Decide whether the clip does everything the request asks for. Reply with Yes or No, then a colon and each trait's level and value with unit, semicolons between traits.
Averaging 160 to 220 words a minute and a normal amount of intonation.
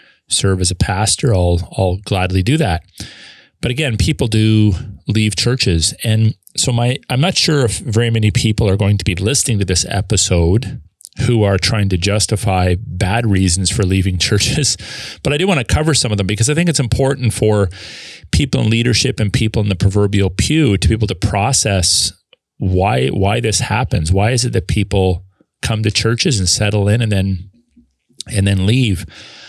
Yes: average, 185 wpm; average, 3.6 semitones